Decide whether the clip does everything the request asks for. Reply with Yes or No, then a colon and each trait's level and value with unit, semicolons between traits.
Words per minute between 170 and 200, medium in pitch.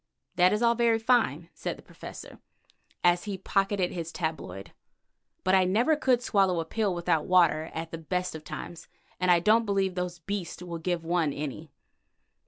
Yes: average, 180 wpm; medium, 180 Hz